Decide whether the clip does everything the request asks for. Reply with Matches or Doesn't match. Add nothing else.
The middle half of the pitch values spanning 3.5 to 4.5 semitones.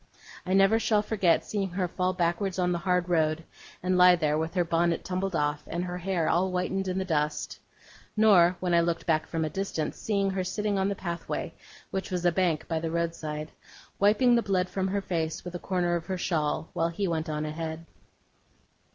Doesn't match